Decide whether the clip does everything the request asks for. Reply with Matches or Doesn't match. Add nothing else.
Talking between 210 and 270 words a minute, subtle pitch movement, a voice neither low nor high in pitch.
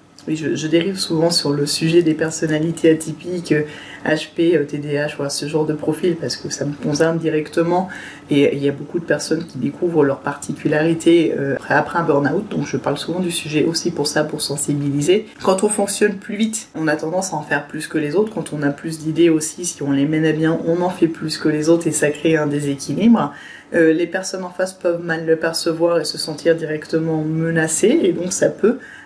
Matches